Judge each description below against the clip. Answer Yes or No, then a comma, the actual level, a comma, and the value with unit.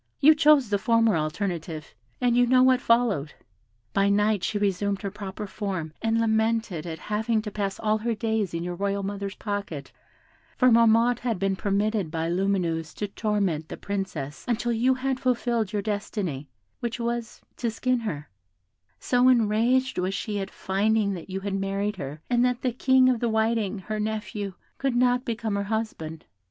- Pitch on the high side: Yes, high, 210 Hz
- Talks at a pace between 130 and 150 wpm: No, average, 175 wpm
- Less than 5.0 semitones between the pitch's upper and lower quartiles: Yes, average, 3.2 semitones